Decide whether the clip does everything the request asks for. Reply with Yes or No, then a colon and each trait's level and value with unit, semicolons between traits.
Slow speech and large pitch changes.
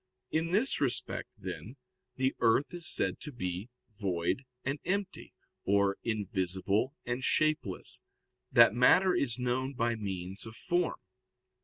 Yes: slow, 130 wpm; wide, 6.8 semitones